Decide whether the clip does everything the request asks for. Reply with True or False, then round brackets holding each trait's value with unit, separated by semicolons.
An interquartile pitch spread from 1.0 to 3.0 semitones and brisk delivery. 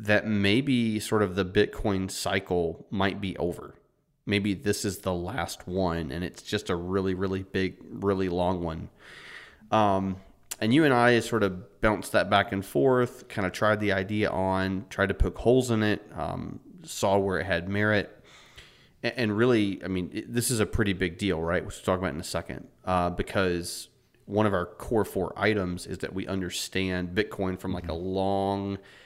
False (2.4 semitones; 190 wpm)